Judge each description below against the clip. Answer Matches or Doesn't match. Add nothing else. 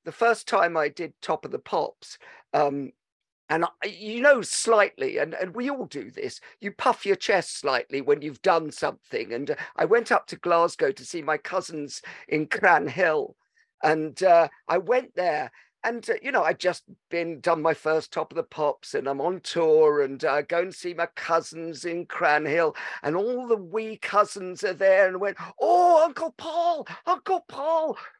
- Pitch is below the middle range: Doesn't match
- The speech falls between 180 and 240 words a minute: Matches